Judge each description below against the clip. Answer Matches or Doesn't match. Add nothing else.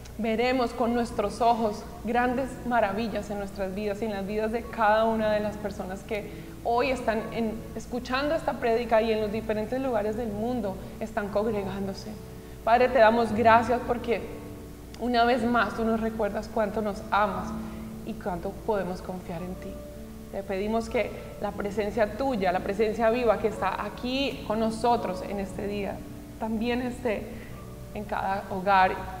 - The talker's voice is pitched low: Doesn't match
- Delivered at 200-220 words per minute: Doesn't match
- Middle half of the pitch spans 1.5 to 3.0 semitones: Matches